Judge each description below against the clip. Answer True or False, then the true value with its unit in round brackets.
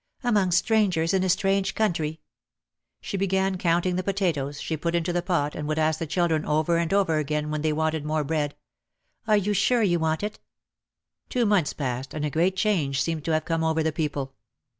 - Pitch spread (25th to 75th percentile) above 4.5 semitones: False (3.7 semitones)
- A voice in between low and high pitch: True (165 Hz)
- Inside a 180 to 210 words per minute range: True (205 wpm)